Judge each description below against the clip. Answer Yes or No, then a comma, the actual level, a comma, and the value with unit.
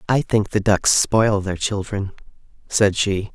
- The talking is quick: No, average, 160 wpm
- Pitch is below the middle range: Yes, low, 100 Hz